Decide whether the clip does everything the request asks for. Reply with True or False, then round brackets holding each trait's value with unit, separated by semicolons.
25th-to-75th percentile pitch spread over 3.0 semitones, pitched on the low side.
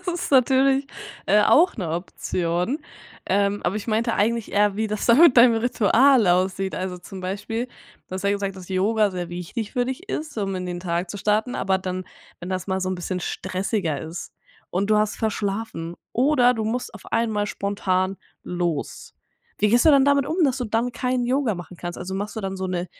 False (4.3 semitones; 205 Hz)